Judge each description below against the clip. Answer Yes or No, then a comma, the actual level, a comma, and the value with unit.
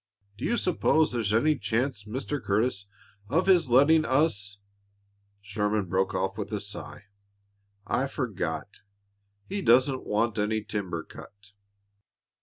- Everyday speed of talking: No, slow, 130 wpm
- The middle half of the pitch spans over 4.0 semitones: Yes, average, 5.3 semitones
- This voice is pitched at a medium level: No, low, 110 Hz